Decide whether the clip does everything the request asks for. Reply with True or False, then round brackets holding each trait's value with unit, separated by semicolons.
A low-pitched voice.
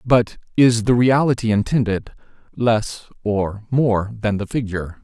True (110 Hz)